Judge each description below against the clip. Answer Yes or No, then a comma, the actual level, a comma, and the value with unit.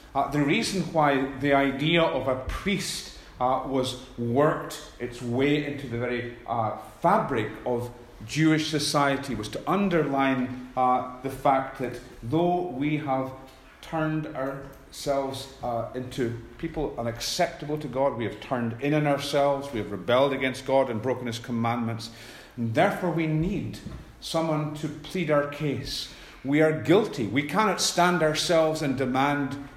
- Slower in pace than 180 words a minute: Yes, average, 145 wpm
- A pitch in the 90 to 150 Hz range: Yes, medium, 140 Hz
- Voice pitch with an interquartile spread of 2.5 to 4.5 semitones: Yes, average, 3.4 semitones